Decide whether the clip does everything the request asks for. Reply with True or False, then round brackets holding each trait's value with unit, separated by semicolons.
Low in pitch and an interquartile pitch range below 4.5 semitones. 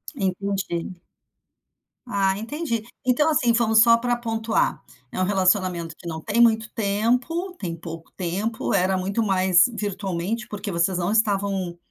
False (200 Hz; 3.7 semitones)